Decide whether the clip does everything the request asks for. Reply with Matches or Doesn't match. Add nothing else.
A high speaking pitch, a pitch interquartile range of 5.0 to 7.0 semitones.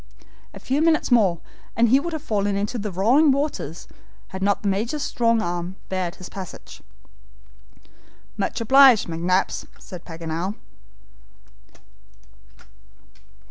Matches